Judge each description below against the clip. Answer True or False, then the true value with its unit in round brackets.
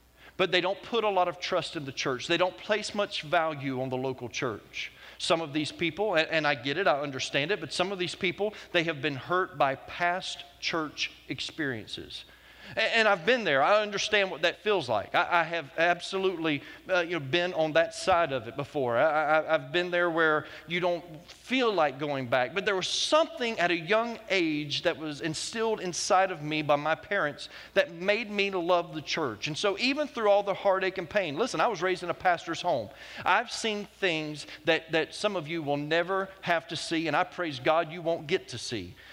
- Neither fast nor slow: False (220 wpm)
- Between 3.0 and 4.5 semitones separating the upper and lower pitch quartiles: True (3.5 semitones)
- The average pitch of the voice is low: False (175 Hz)